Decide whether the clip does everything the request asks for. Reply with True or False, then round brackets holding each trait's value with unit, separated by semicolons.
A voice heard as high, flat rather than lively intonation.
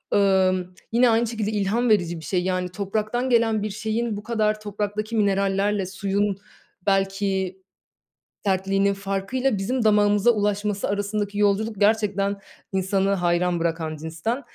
True (200 Hz; 1.9 semitones)